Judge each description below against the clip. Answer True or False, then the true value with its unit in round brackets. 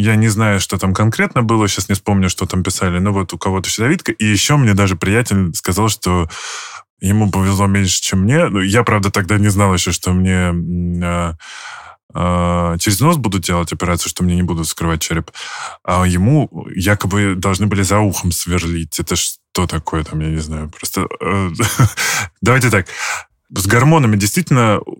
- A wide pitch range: False (3.0 semitones)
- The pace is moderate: False (180 wpm)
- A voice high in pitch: False (95 Hz)